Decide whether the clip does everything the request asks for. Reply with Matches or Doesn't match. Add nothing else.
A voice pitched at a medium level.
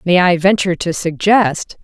Matches